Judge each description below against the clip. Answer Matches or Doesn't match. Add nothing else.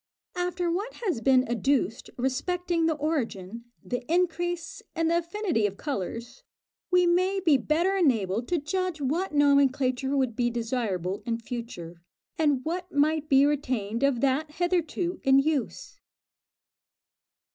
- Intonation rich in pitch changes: Matches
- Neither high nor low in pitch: Doesn't match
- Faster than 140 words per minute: Doesn't match